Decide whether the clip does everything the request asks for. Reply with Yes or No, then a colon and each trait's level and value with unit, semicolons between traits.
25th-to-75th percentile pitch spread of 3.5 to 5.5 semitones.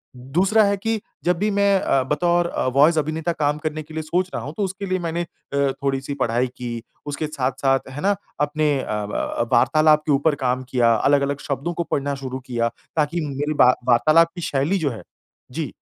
Yes: average, 4.2 semitones